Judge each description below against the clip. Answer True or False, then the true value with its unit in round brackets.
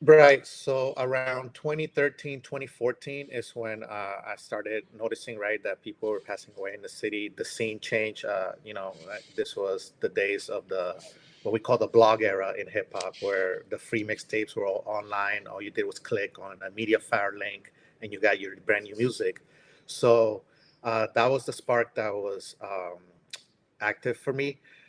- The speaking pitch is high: False (140 Hz)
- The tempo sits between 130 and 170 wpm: False (185 wpm)